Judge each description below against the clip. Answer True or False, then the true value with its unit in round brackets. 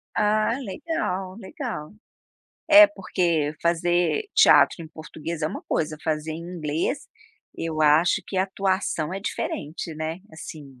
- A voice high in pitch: False (170 Hz)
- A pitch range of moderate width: True (3.6 semitones)